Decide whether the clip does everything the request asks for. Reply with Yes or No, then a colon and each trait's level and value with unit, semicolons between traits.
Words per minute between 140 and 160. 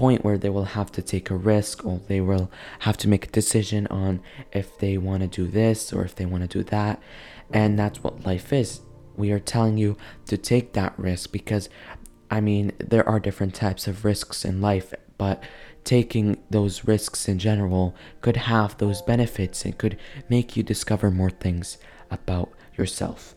No: average, 190 wpm